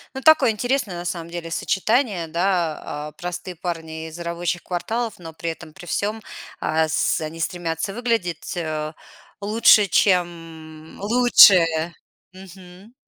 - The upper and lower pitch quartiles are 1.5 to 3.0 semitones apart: No, average, 3.7 semitones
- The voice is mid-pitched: Yes, medium, 175 Hz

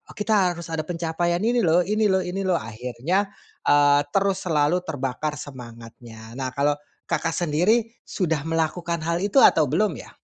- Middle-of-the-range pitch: Yes, medium, 165 Hz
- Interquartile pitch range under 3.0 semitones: No, average, 4.5 semitones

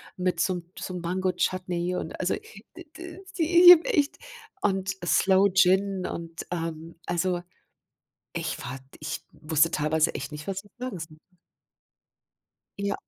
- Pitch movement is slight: No, average, 3.2 semitones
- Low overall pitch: No, medium, 180 Hz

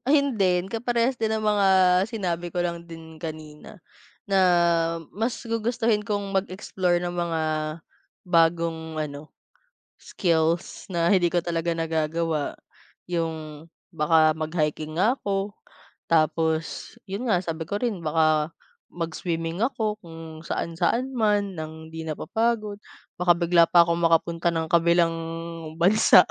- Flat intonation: No, average, 3.8 semitones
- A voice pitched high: No, medium, 170 Hz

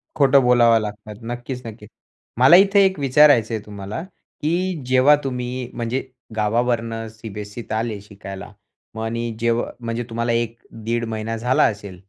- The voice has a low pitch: Yes, low, 115 Hz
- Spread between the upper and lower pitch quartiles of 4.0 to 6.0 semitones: No, narrow, 2.6 semitones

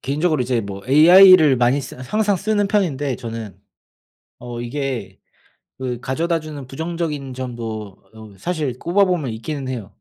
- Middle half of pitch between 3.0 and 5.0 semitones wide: No, wide, 5.5 semitones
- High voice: No, low, 135 Hz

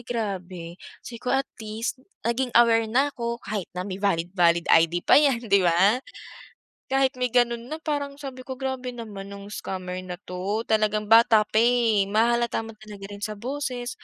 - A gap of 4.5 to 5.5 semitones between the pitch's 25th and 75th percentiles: No, average, 3.8 semitones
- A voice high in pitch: Yes, high, 225 Hz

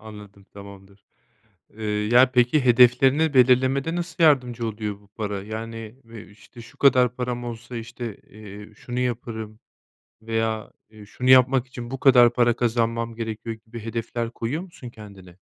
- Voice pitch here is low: Yes, low, 115 Hz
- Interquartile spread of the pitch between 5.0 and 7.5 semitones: No, narrow, 2.5 semitones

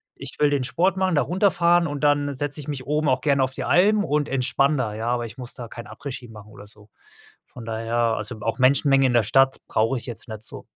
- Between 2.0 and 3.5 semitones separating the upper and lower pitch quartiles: No, average, 4.2 semitones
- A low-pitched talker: Yes, low, 130 Hz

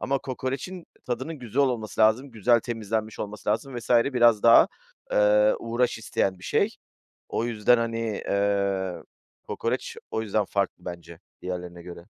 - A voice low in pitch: Yes, low, 110 Hz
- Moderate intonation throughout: Yes, average, 3.5 semitones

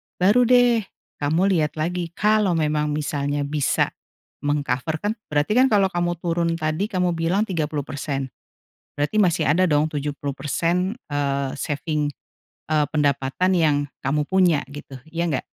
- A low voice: No, medium, 155 Hz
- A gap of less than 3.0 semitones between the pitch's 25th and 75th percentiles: No, average, 3.7 semitones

